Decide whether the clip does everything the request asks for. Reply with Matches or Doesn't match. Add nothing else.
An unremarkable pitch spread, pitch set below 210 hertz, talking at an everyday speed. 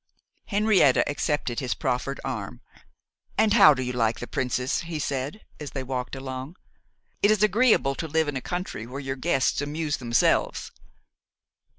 Matches